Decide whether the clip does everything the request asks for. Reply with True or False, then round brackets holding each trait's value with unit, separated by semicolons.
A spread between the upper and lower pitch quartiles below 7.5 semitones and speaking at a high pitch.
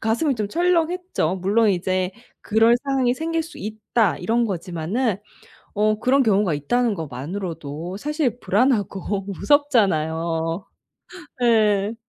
True (5.6 semitones; 210 Hz)